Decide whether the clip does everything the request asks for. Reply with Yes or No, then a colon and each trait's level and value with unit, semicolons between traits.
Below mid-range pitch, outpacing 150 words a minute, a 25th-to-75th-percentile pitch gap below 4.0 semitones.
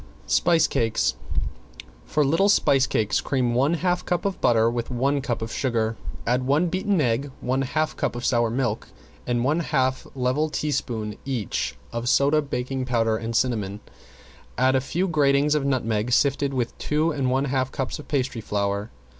Yes: low, 130 Hz; average, 170 wpm; average, 3.6 semitones